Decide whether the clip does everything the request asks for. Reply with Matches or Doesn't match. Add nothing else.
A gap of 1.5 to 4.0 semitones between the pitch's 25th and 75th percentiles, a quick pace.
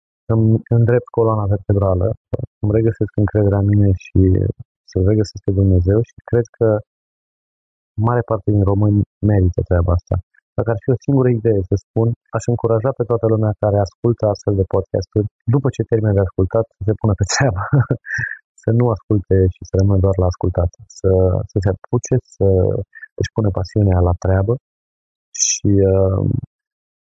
Doesn't match